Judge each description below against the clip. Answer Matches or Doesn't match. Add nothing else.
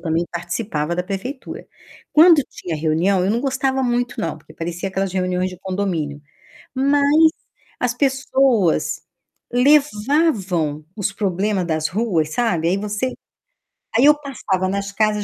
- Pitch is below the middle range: Doesn't match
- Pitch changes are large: Matches